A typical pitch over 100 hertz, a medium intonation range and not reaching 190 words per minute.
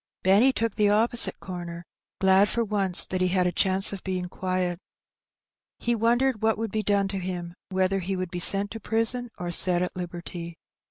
No: high, 190 Hz; average, 3.1 semitones; average, 195 wpm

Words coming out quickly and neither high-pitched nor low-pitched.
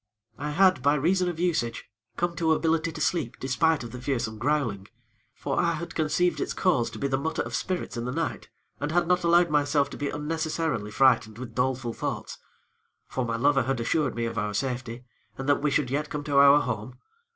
Yes: fast, 210 wpm; medium, 145 Hz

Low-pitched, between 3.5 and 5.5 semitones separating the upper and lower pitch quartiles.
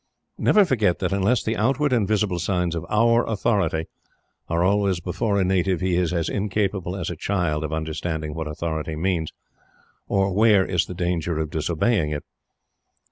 Yes: very low, 90 Hz; average, 3.9 semitones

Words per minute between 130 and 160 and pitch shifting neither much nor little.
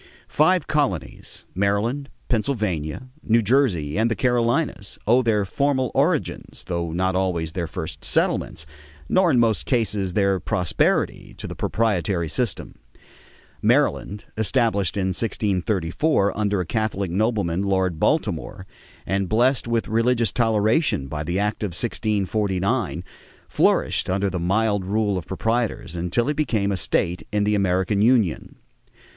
Yes: slow, 135 wpm; average, 4.1 semitones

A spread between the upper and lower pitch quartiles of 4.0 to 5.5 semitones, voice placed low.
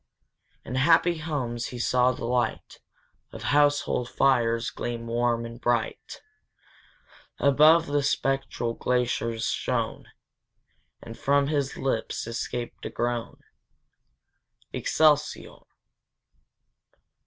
No: average, 3.5 semitones; low, 125 Hz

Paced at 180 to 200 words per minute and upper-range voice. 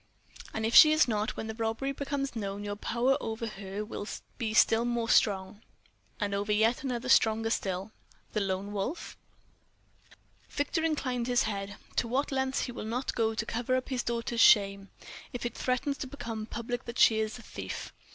Yes: average, 185 wpm; high, 225 Hz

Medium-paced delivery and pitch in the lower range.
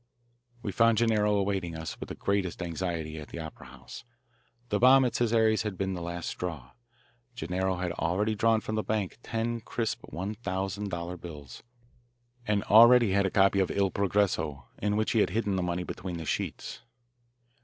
Yes: average, 180 wpm; very low, 95 Hz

